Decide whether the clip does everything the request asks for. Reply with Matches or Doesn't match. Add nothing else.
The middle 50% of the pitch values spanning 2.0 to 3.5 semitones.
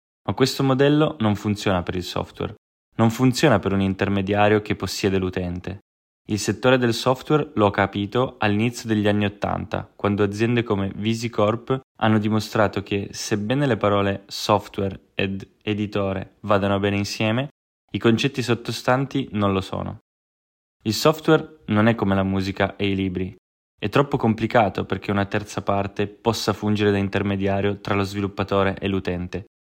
Matches